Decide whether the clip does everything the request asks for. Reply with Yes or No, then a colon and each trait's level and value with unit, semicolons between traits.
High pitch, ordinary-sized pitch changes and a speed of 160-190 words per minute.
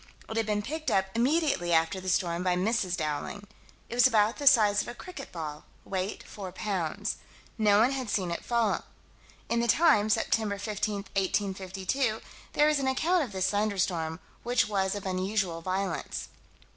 Yes: high, 205 Hz; average, 3.9 semitones; average, 170 wpm